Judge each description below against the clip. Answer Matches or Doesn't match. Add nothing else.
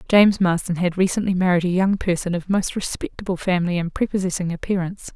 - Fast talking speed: Doesn't match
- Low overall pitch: Doesn't match